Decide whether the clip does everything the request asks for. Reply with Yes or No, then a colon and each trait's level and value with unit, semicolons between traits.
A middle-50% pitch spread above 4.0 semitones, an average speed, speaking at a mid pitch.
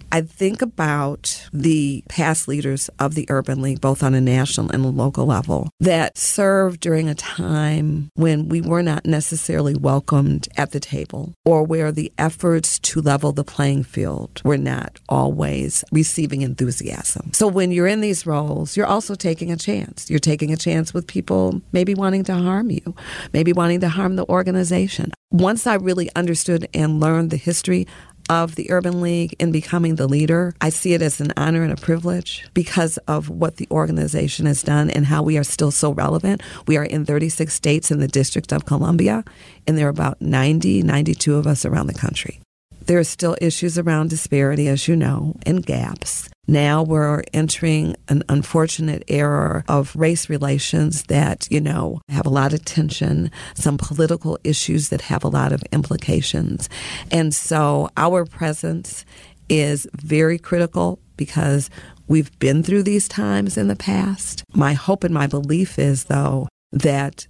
No: average, 3.0 semitones; average, 175 wpm; medium, 155 Hz